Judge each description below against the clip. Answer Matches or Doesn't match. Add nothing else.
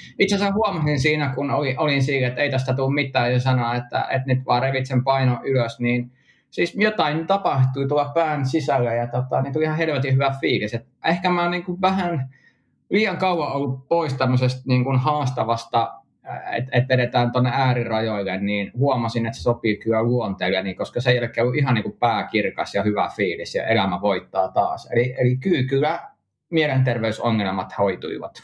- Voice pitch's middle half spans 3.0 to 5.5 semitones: Matches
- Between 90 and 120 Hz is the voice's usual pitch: Doesn't match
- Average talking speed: Doesn't match